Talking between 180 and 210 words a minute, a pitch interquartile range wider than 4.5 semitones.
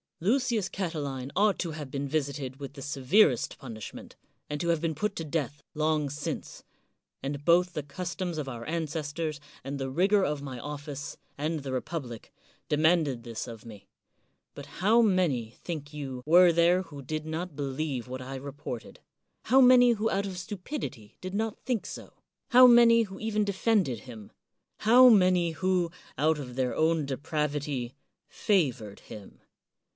No: average, 160 wpm; average, 5.2 semitones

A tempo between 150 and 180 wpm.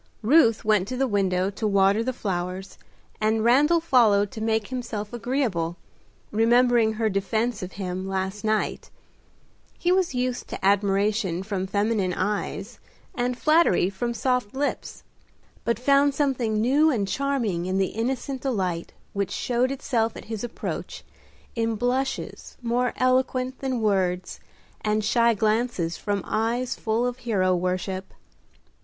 No: average, 140 wpm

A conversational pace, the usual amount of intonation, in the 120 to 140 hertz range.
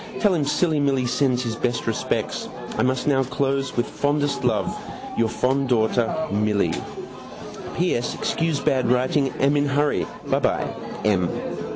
Yes: average, 150 wpm; average, 3.2 semitones; low, 135 Hz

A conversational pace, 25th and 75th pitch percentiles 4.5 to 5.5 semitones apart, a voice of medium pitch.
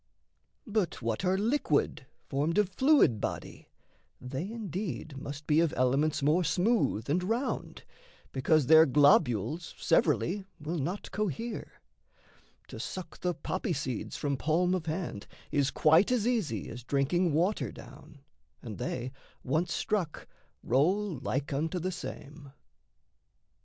No: slow, 130 wpm; average, 5.1 semitones; medium, 160 Hz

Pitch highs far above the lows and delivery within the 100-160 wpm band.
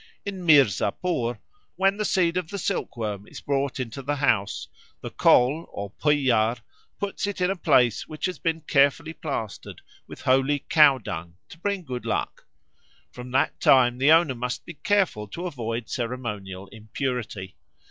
Yes: wide, 6.0 semitones; average, 155 wpm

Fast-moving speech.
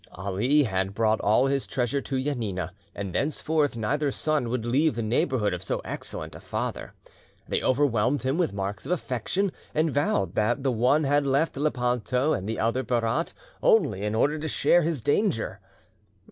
No: average, 175 wpm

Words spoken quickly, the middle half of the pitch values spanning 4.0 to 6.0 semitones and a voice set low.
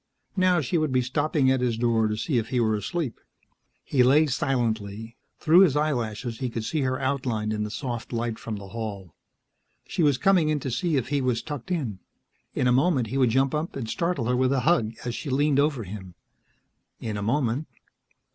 Yes: fast, 210 wpm; average, 4.6 semitones; low, 125 Hz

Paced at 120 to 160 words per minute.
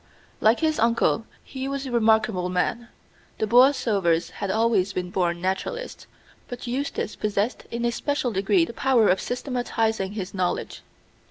Yes: average, 150 wpm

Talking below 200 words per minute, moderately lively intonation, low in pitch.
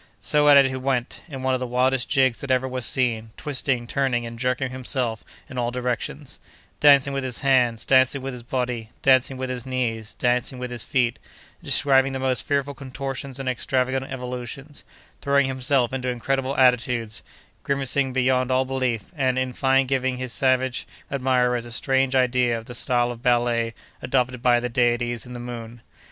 No: average, 180 wpm; narrow, 1.5 semitones; low, 130 Hz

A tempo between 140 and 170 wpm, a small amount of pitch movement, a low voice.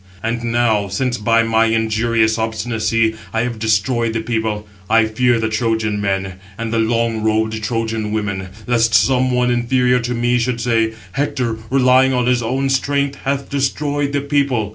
Yes: average, 165 wpm; narrow, 2.1 semitones; low, 115 Hz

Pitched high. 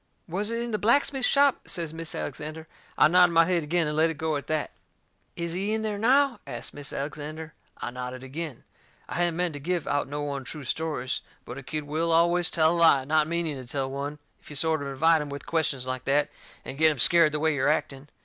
No: medium, 155 Hz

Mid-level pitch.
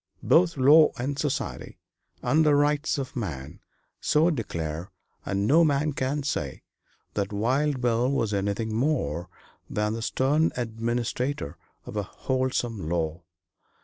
No: low, 125 Hz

